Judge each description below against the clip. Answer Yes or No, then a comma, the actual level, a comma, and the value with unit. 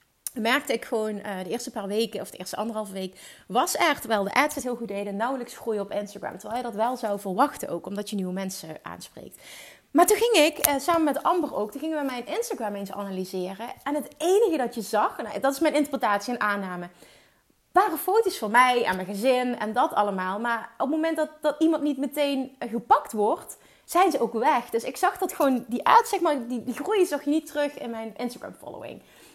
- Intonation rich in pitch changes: Yes, wide, 6.0 semitones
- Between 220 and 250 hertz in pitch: Yes, high, 245 Hz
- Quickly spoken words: Yes, fast, 225 wpm